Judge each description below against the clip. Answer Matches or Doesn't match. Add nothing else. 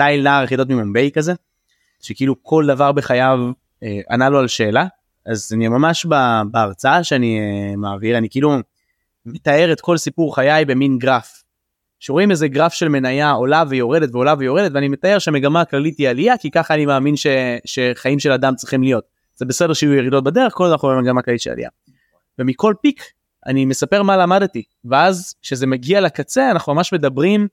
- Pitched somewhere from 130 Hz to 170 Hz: Matches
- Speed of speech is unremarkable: Doesn't match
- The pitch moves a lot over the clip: Doesn't match